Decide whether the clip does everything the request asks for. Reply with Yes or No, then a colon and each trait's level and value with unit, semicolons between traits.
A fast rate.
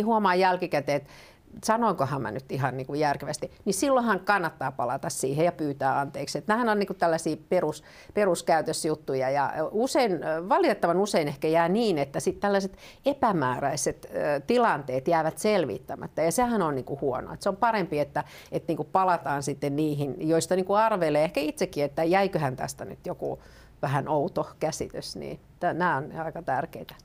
Yes: fast, 165 wpm